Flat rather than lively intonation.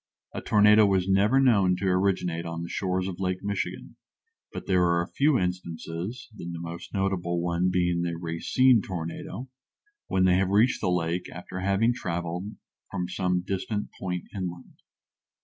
Yes: narrow, 2.3 semitones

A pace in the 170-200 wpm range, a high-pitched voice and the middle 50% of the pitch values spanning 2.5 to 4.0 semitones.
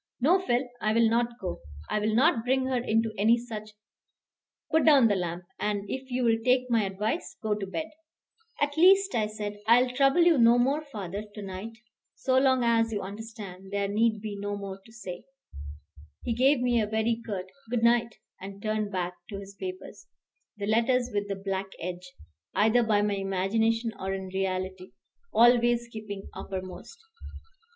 Yes: average, 180 wpm; high, 220 Hz; average, 3.5 semitones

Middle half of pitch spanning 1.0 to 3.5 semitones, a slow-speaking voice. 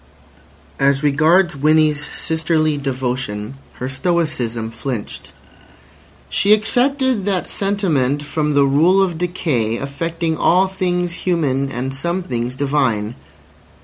No: average, 4.9 semitones; slow, 110 wpm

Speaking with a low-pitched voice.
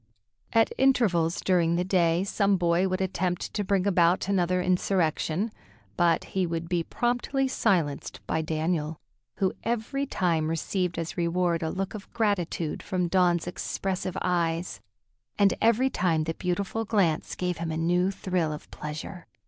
No: medium, 180 Hz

